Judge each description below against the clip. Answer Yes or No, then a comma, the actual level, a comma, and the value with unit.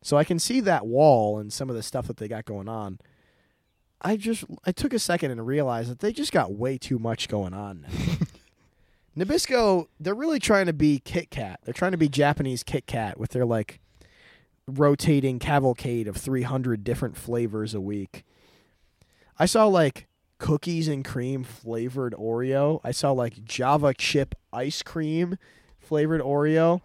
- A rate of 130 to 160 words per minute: No, average, 170 wpm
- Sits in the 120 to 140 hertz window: Yes, low, 135 Hz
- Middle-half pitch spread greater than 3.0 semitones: Yes, wide, 5.4 semitones